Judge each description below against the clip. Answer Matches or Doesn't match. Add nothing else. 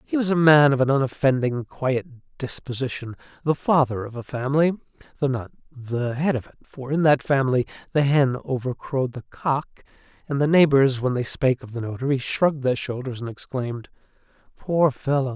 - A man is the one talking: Matches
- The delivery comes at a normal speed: Matches